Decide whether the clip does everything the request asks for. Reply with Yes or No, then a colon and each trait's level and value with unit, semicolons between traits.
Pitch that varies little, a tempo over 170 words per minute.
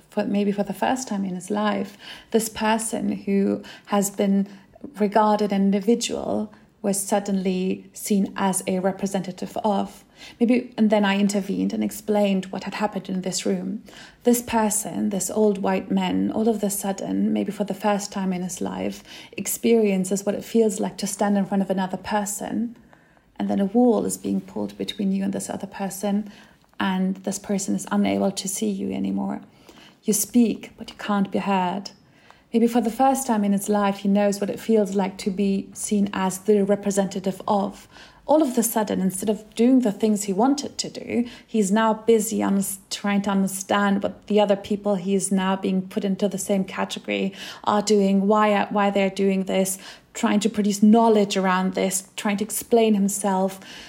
Yes: narrow, 1.9 semitones; average, 185 wpm